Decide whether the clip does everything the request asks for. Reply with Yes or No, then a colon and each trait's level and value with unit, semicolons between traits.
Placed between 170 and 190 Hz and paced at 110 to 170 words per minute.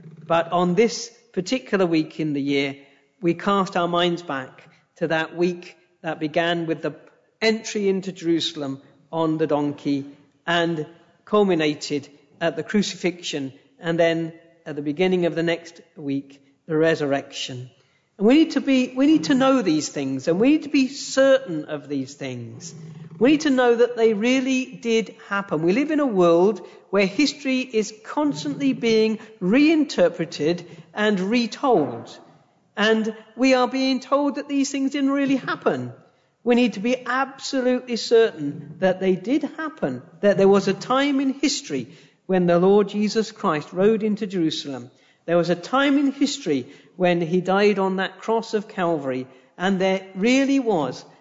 Yes: medium, 185 Hz; average, 160 wpm